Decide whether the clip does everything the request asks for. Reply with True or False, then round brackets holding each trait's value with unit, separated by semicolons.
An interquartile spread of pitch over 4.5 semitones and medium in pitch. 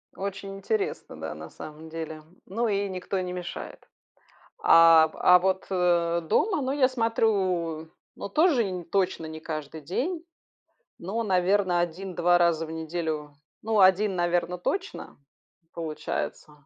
False (3.6 semitones; 180 Hz)